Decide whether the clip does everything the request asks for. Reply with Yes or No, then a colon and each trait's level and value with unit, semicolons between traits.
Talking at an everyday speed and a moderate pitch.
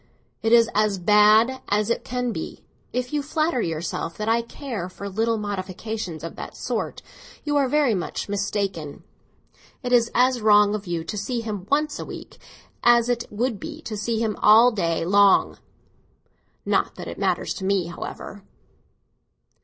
No: average, 170 wpm; high, 215 Hz